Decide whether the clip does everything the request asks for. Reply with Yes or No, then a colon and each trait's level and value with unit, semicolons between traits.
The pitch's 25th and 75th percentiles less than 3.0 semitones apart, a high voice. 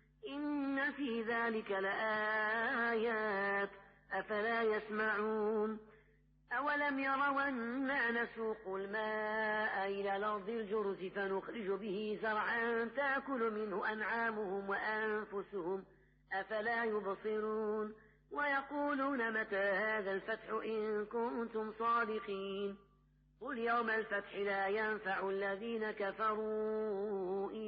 Yes: narrow, 2.5 semitones; high, 215 Hz